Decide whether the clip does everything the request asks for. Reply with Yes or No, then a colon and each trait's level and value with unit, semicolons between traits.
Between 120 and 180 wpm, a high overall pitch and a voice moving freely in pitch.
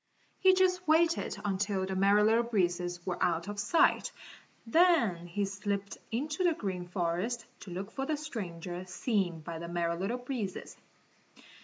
Yes: average, 155 wpm; high, 200 Hz; wide, 5.7 semitones